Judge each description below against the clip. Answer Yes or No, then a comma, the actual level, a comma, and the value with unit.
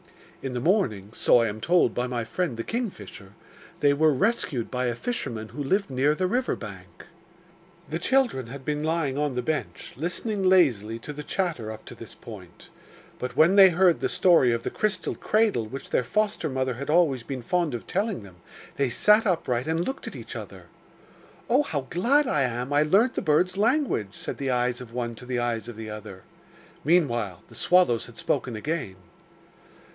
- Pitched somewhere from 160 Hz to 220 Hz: No, medium, 140 Hz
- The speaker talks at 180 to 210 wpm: Yes, average, 195 wpm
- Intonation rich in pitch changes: Yes, wide, 7.2 semitones